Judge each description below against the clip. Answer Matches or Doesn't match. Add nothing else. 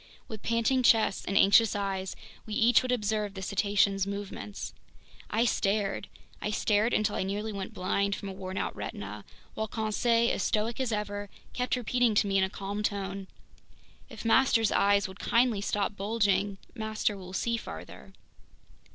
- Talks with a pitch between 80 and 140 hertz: Doesn't match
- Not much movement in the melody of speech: Matches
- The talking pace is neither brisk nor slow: Matches